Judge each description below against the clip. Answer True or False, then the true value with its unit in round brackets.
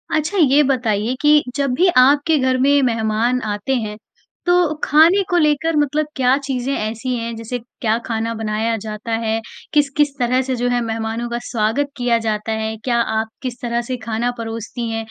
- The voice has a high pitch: True (245 Hz)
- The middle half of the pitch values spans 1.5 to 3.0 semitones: False (3.9 semitones)